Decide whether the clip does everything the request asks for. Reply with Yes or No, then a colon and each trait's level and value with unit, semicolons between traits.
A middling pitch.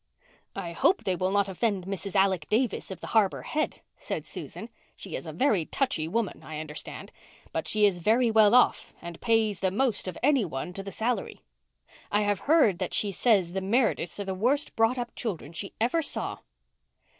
No: high, 205 Hz